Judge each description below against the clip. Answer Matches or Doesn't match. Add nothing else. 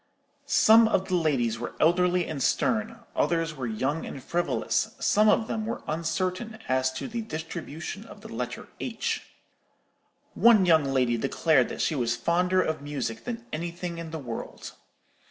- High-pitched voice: Doesn't match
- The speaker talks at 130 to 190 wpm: Matches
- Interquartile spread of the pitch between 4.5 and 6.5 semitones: Matches